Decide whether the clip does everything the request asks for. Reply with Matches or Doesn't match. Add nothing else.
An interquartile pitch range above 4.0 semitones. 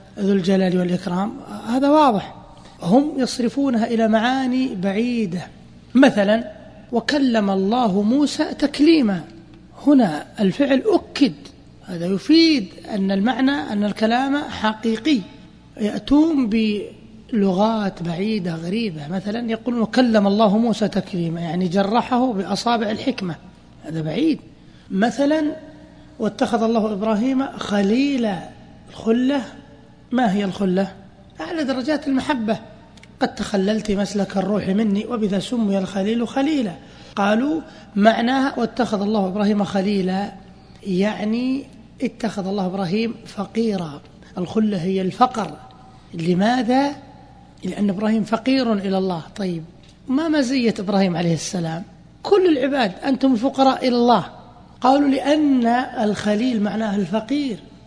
Matches